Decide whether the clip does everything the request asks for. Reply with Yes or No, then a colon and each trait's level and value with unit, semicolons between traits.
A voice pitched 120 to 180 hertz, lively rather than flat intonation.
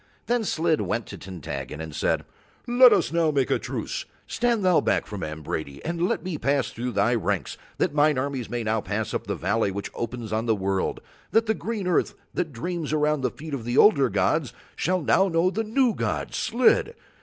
Yes: medium, 140 Hz; wide, 8.7 semitones